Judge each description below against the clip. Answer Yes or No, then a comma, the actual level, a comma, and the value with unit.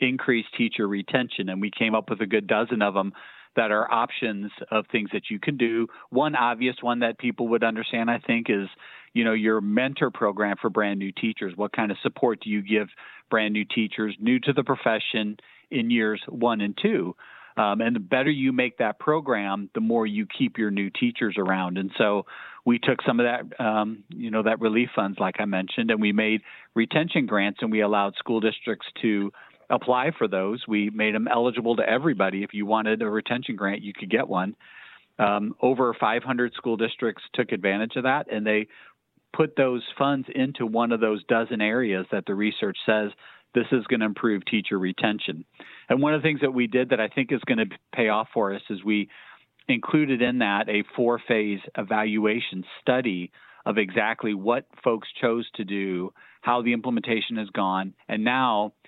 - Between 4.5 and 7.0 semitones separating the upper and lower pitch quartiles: No, average, 2.8 semitones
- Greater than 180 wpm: Yes, average, 200 wpm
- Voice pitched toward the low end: Yes, low, 110 Hz